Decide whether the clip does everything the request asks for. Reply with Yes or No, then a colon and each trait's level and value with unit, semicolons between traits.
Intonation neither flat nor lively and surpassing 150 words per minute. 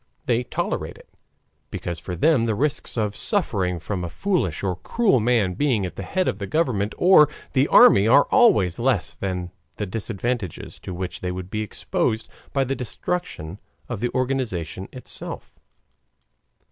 No: wide, 6.3 semitones; average, 160 wpm